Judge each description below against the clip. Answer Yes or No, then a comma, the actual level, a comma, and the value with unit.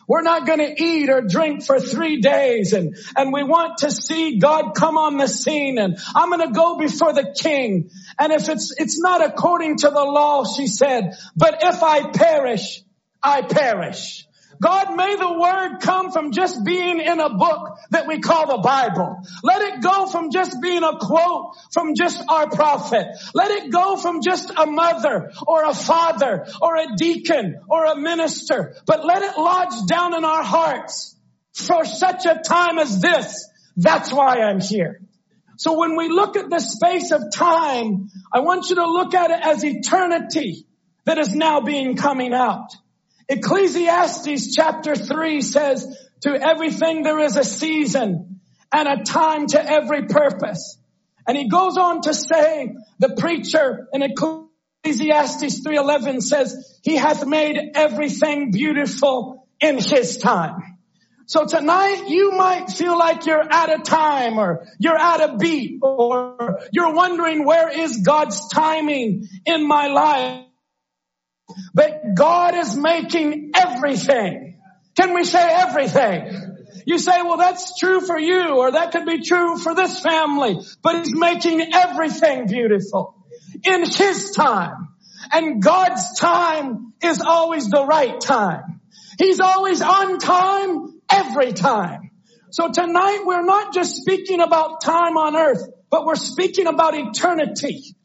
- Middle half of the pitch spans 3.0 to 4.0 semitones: No, average, 4.4 semitones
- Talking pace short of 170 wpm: Yes, average, 155 wpm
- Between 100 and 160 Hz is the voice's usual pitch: No, very high, 310 Hz